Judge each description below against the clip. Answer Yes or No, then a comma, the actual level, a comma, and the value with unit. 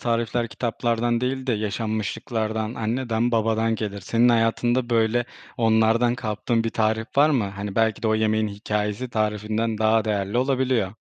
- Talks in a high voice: No, low, 110 Hz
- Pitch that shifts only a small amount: Yes, narrow, 1.7 semitones